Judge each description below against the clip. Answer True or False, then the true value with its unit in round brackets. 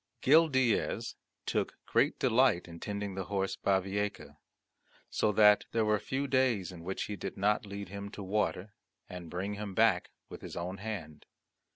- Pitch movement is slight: True (2.2 semitones)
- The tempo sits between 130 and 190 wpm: True (170 wpm)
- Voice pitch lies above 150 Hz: False (100 Hz)